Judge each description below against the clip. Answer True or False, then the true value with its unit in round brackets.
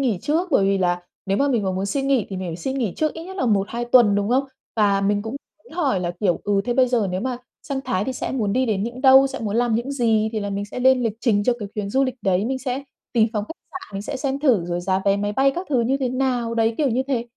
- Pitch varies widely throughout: False (4.6 semitones)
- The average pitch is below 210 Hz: False (235 Hz)